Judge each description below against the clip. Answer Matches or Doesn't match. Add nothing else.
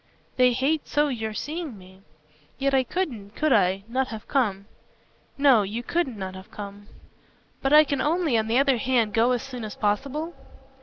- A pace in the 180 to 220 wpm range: Matches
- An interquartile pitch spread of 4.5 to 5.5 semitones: Matches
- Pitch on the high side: Matches